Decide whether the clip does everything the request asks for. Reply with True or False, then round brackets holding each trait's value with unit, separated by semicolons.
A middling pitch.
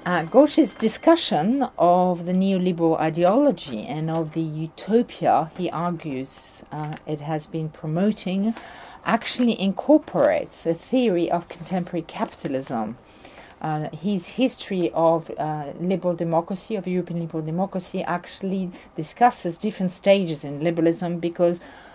True (175 Hz)